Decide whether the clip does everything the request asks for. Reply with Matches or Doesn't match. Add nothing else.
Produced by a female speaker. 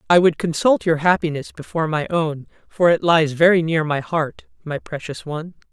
Matches